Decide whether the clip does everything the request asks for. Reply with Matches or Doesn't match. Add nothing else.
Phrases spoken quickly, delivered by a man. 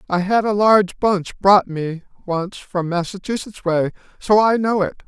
Doesn't match